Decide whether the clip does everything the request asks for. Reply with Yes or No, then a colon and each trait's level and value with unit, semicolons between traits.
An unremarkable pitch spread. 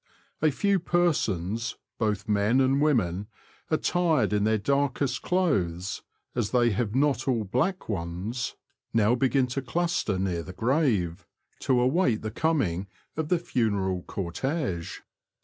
No: wide, 6.1 semitones